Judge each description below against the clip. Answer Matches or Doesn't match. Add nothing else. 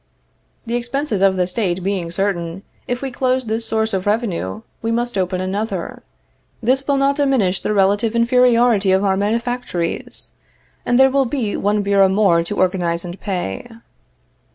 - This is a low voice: Doesn't match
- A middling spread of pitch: Matches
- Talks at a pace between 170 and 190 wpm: Doesn't match